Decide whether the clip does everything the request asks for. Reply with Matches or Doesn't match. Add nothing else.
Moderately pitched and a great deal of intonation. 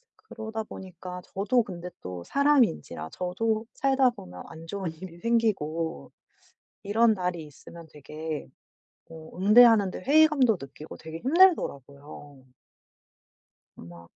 Matches